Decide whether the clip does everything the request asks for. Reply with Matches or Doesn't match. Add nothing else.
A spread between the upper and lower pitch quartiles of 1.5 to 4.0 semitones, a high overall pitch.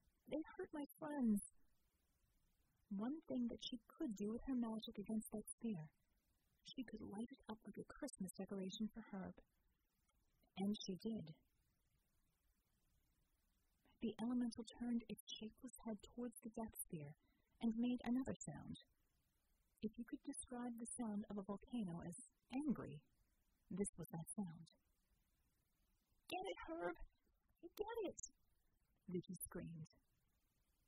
Doesn't match